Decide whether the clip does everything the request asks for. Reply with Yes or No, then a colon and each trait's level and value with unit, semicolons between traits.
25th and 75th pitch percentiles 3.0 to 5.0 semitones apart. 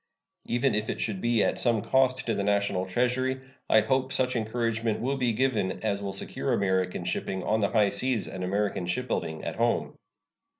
Yes: average, 4.0 semitones